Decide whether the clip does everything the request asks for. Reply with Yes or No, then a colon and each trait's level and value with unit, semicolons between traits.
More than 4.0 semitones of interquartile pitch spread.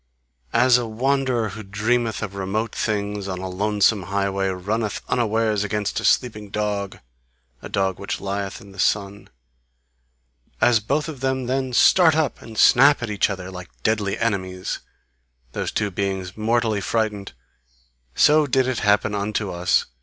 No: average, 3.1 semitones